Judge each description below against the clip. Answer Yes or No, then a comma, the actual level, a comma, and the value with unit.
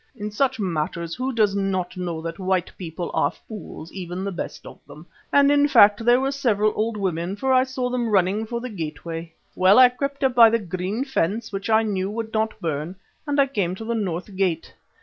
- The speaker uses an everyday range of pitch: Yes, average, 4.8 semitones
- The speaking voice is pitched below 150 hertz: No, high, 205 Hz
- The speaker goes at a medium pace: No, fast, 215 wpm